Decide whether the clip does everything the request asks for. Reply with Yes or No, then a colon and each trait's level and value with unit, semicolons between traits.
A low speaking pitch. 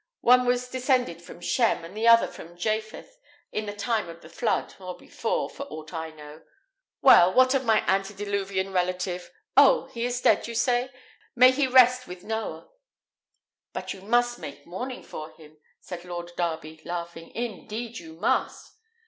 No: high, 205 Hz